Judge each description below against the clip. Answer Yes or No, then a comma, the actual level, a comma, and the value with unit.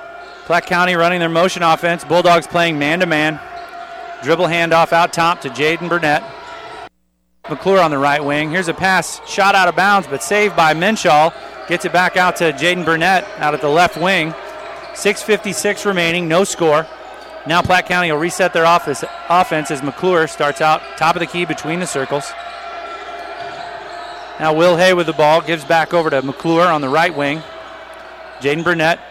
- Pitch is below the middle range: No, medium, 170 Hz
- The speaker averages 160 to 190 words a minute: Yes, average, 175 wpm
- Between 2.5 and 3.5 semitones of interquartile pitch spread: Yes, average, 2.9 semitones